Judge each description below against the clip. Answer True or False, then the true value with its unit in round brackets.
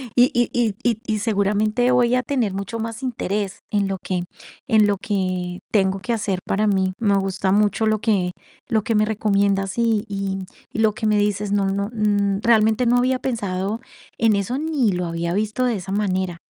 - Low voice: False (210 Hz)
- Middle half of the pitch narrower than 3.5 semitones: True (2.7 semitones)